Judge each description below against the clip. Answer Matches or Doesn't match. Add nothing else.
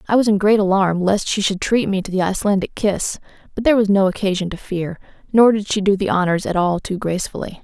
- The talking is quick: Matches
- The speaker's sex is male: Doesn't match